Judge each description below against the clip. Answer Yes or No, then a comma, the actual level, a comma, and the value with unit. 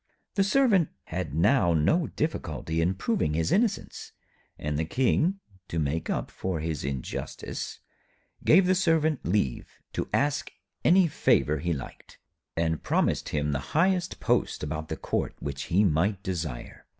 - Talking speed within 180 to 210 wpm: No, average, 150 wpm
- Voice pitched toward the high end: No, very low, 90 Hz